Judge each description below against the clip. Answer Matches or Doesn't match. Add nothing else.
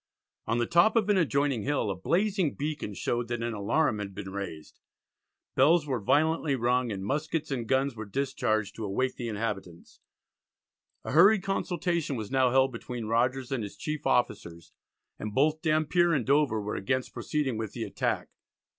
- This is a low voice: Matches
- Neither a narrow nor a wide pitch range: Doesn't match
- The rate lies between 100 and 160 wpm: Doesn't match